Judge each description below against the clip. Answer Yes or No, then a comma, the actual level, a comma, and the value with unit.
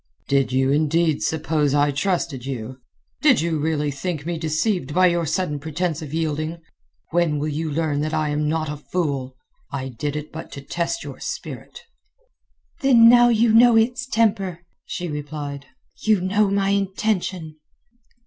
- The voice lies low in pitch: No, medium, 160 Hz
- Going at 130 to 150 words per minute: No, average, 160 wpm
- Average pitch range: Yes, average, 4.0 semitones